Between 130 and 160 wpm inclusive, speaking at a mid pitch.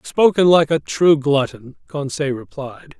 Yes: average, 140 wpm; medium, 145 Hz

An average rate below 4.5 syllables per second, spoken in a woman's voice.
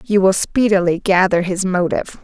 No: 5.2 syllables/s; female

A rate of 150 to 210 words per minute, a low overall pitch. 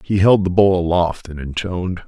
Yes: fast, 205 wpm; very low, 90 Hz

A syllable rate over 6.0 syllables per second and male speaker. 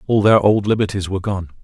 Yes: 6.5 syllables/s; male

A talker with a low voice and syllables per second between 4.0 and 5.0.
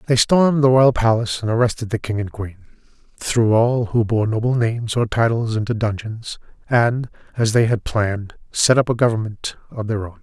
No: low, 115 Hz; 5.3 syllables/s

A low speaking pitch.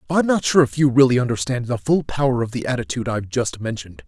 Yes: low, 125 Hz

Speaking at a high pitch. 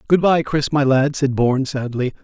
No: medium, 140 Hz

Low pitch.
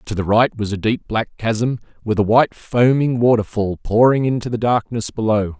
Yes: low, 115 Hz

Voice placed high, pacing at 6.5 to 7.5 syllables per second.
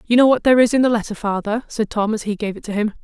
Yes: high, 220 Hz; 7.1 syllables/s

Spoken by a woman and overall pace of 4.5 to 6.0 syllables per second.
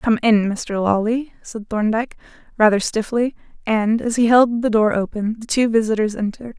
Yes: female; 5.1 syllables/s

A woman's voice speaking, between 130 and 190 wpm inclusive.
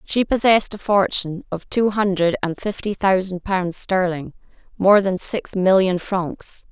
Yes: female; average, 150 wpm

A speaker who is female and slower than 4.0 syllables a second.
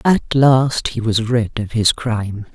Yes: female; 3.8 syllables/s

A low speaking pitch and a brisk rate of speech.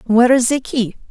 No: high, 240 Hz; fast, 220 wpm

